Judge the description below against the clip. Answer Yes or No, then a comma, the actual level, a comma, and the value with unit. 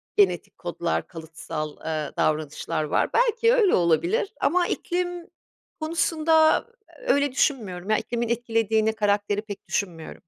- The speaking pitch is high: Yes, high, 225 Hz